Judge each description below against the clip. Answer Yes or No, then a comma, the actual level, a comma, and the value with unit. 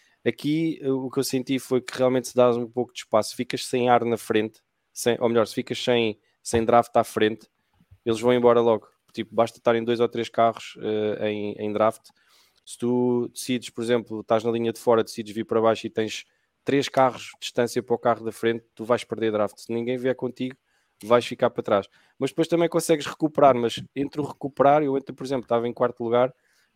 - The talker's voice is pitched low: Yes, low, 120 Hz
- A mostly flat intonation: Yes, narrow, 2.1 semitones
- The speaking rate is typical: No, fast, 225 wpm